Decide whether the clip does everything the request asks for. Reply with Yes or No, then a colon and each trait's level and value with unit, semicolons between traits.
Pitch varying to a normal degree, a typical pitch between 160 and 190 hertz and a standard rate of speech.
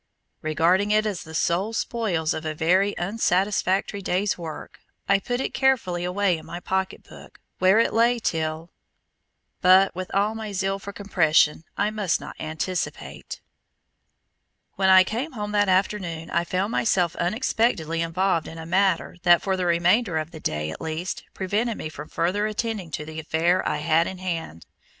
Yes: average, 3.7 semitones; medium, 185 Hz; average, 170 wpm